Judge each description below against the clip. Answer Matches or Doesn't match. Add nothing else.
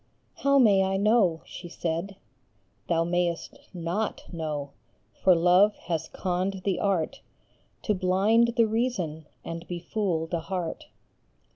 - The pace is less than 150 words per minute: Matches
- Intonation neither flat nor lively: Matches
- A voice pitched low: Doesn't match